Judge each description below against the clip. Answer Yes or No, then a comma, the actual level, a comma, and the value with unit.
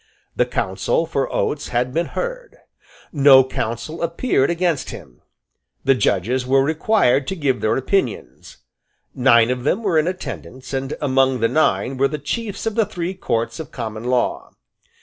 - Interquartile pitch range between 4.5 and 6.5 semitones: Yes, wide, 5.4 semitones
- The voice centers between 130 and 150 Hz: Yes, low, 135 Hz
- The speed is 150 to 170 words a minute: Yes, average, 160 wpm